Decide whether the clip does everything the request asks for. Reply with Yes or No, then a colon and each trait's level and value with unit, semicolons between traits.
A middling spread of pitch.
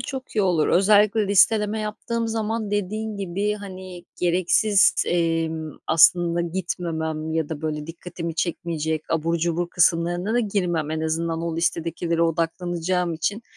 Yes: average, 3.5 semitones